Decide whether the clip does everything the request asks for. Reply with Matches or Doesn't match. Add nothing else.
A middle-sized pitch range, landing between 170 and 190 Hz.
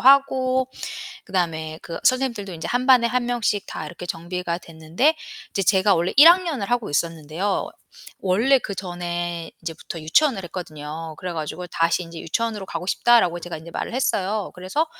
Doesn't match